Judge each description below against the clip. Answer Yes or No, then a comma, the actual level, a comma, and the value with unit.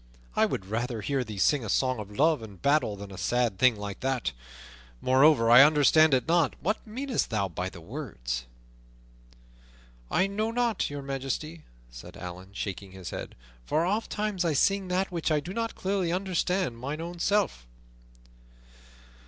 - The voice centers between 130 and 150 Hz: Yes, medium, 140 Hz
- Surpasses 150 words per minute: Yes, average, 165 wpm